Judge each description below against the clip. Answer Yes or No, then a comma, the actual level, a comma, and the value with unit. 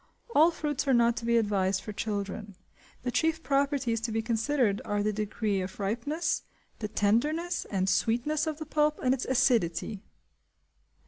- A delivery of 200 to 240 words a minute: No, average, 165 wpm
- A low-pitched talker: No, high, 235 Hz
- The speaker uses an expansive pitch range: Yes, wide, 5.8 semitones